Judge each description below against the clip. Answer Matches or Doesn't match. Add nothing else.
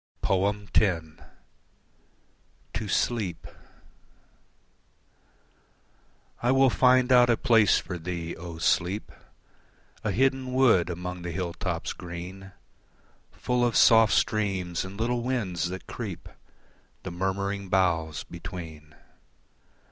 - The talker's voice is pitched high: Doesn't match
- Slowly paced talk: Matches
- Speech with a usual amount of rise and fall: Matches